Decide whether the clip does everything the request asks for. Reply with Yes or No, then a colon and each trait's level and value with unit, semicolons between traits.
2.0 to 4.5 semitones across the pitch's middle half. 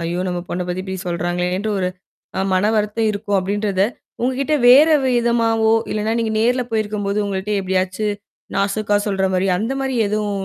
Yes: average, 2.8 semitones